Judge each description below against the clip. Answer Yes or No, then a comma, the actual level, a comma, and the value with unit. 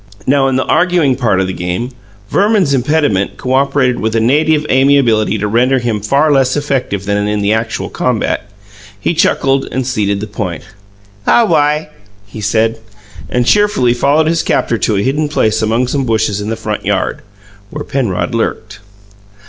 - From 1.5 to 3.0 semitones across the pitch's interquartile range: No, average, 4.8 semitones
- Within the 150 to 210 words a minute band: Yes, average, 170 wpm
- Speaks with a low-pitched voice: Yes, low, 125 Hz